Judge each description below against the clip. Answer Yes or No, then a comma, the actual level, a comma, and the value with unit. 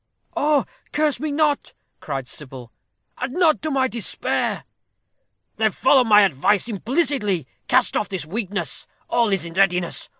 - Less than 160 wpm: Yes, average, 140 wpm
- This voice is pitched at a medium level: No, high, 210 Hz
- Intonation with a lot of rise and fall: Yes, wide, 7.9 semitones